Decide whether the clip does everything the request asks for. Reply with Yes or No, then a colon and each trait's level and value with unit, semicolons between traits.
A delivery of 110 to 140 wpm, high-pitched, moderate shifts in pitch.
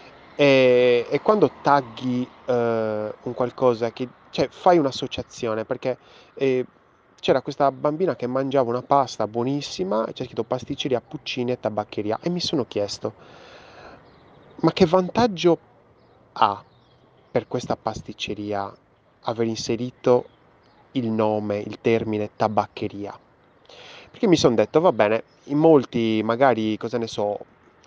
No: average, 125 wpm; low, 125 Hz; average, 3.8 semitones